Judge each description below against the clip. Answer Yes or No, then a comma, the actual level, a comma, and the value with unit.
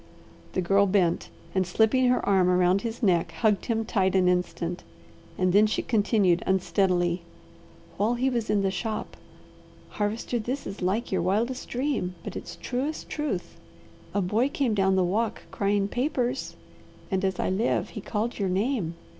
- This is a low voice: No, high, 200 Hz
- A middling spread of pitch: Yes, average, 4.0 semitones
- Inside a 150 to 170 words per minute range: Yes, average, 165 wpm